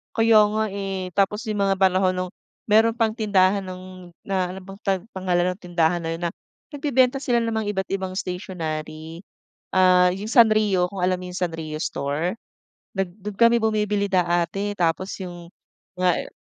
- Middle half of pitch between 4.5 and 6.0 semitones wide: No, average, 2.7 semitones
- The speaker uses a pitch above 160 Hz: Yes, medium, 185 Hz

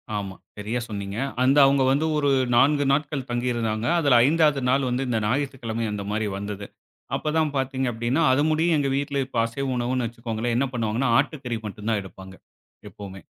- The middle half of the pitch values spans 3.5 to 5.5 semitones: Yes, average, 4.2 semitones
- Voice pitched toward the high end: No, low, 125 Hz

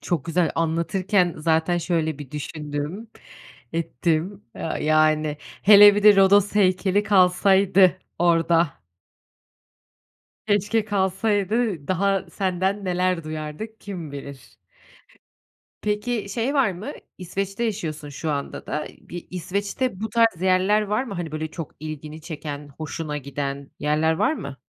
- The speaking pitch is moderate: Yes, medium, 180 Hz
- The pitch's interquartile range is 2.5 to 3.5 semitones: No, average, 4.6 semitones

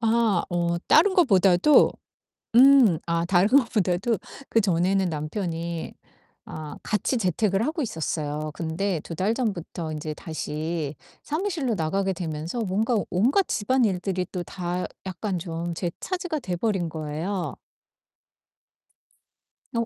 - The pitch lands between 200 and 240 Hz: No, medium, 185 Hz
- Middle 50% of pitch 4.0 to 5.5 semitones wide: Yes, average, 5.1 semitones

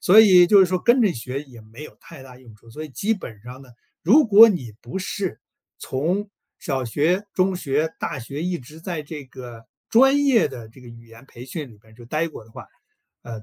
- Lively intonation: Yes, wide, 7.4 semitones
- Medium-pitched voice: Yes, medium, 150 Hz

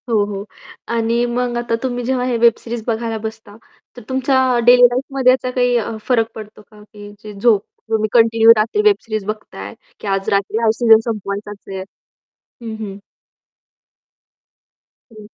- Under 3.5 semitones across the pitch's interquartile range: Yes, narrow, 2.6 semitones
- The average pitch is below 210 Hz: No, high, 225 Hz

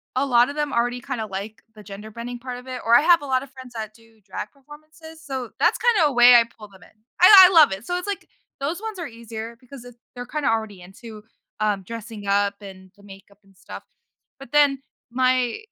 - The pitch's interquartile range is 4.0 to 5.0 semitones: Yes, average, 4.7 semitones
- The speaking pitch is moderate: No, high, 240 Hz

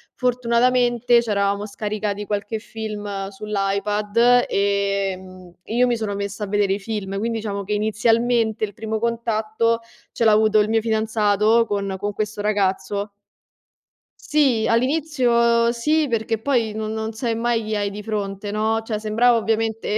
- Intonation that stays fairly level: Yes, narrow, 2.2 semitones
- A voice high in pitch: Yes, high, 215 Hz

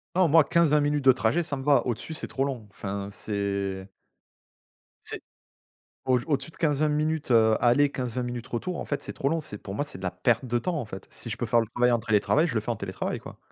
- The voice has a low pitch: Yes, low, 125 Hz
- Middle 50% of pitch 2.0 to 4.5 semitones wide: No, average, 5.0 semitones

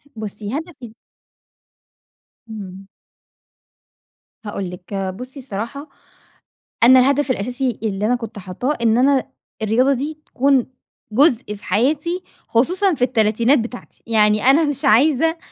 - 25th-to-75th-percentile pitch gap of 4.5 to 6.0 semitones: Yes, average, 4.8 semitones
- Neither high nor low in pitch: No, high, 245 Hz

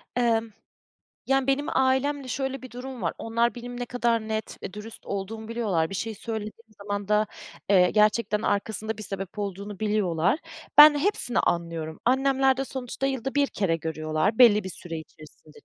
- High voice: Yes, high, 220 Hz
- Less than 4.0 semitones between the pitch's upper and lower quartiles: No, average, 4.5 semitones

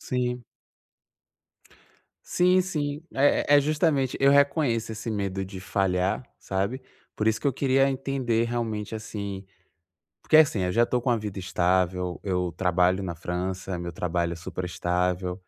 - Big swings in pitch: Yes, wide, 6.3 semitones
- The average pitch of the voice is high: No, low, 105 Hz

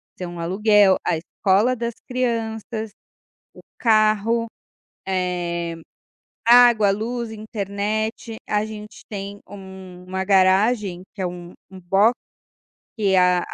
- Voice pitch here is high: Yes, high, 205 Hz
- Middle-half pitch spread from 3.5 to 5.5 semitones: No, average, 2.9 semitones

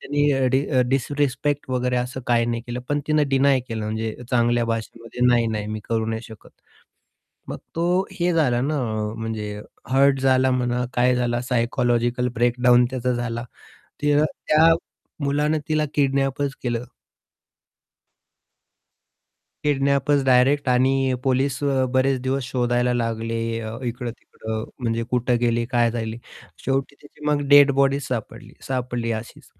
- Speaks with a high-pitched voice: No, low, 125 Hz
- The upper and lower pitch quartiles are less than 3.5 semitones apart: Yes, average, 2.7 semitones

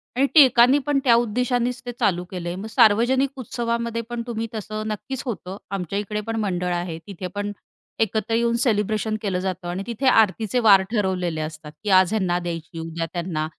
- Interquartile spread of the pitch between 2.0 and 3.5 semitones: No, average, 4.5 semitones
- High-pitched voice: Yes, high, 210 Hz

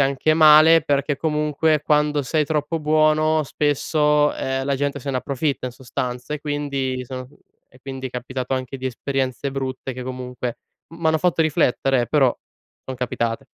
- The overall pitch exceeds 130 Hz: Yes, medium, 140 Hz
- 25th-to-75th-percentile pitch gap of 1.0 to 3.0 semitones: Yes, average, 2.7 semitones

